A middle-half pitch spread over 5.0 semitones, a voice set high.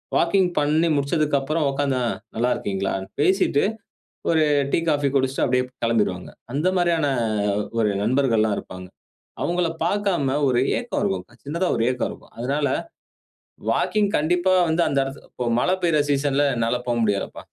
No: wide, 5.4 semitones; medium, 140 Hz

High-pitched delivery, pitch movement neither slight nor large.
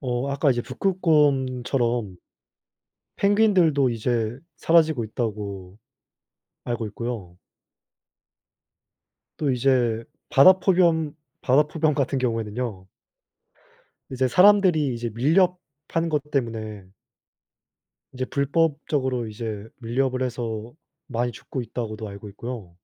No: low, 125 Hz; average, 4.8 semitones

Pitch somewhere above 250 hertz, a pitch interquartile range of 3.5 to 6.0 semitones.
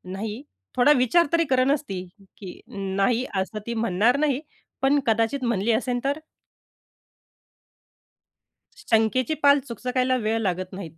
No: high, 235 Hz; average, 4.2 semitones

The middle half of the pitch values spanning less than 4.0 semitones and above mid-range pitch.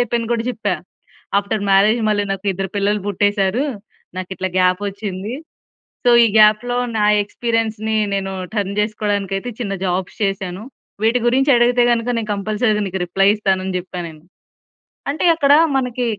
Yes: average, 2.8 semitones; high, 205 Hz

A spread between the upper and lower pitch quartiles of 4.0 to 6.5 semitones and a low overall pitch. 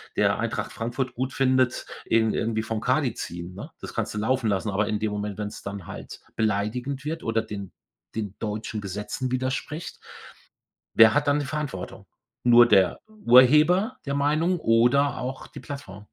Yes: average, 4.9 semitones; low, 120 Hz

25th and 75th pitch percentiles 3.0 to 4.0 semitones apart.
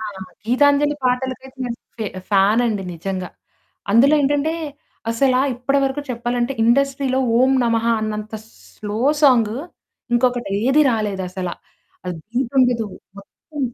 Yes: average, 3.7 semitones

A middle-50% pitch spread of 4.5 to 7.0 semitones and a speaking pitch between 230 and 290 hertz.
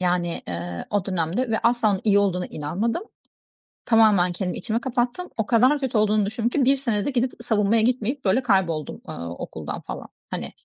No: average, 5.0 semitones; high, 215 Hz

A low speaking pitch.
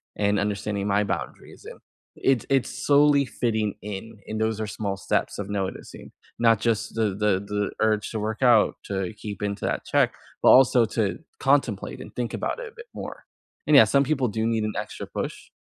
Yes: low, 110 Hz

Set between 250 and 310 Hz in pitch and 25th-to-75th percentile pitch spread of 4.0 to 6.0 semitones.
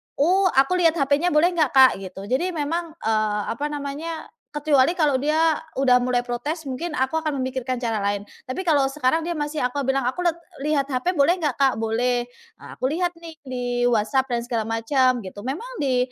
Yes: very high, 275 Hz; average, 4.3 semitones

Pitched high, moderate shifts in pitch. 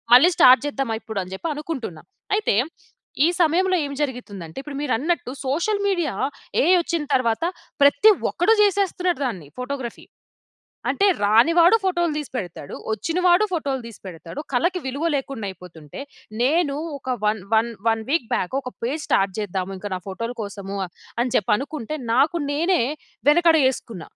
No: very high, 265 Hz; wide, 7.5 semitones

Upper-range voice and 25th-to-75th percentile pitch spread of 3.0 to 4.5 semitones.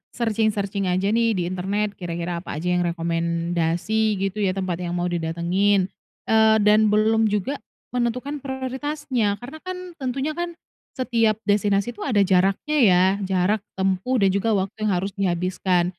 Yes: high, 200 Hz; average, 4.0 semitones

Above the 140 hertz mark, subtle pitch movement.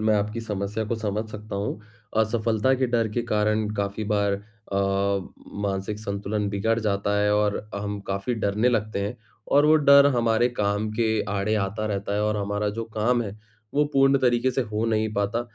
No: low, 105 Hz; narrow, 2.0 semitones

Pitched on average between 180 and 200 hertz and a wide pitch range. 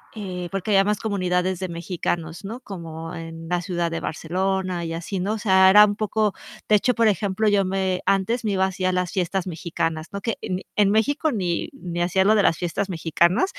No: high, 190 Hz; average, 2.9 semitones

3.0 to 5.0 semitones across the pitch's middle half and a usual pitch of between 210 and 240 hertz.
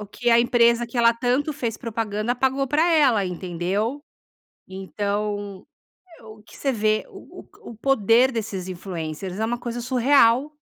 Yes: average, 3.5 semitones; high, 230 Hz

